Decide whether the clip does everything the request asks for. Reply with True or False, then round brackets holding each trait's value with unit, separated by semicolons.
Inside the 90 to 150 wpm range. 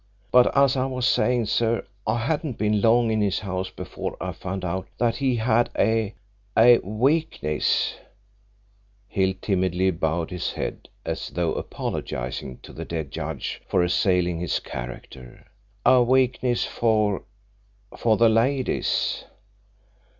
True (135 wpm)